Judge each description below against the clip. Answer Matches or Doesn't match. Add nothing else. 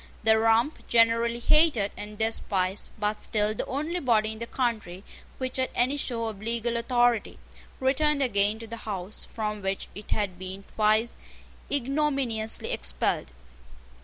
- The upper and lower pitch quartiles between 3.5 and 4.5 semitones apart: Doesn't match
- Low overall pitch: Doesn't match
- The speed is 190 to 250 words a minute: Doesn't match